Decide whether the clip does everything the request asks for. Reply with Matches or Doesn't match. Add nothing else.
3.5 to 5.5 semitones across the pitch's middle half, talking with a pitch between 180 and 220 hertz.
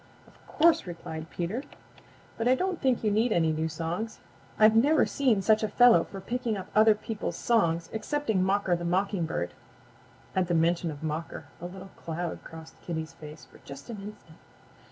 Matches